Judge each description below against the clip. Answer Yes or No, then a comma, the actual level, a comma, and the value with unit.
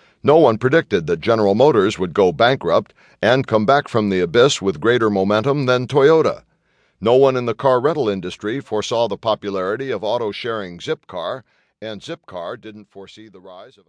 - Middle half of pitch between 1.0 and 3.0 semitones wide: No, average, 3.7 semitones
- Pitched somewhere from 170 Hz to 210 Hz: No, low, 110 Hz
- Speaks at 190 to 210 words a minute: No, average, 175 wpm